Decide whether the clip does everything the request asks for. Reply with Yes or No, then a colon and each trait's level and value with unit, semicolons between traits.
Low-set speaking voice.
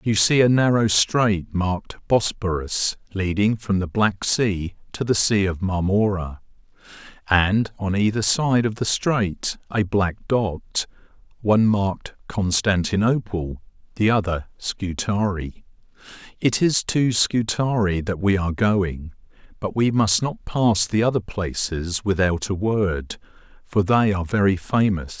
Yes: low, 100 Hz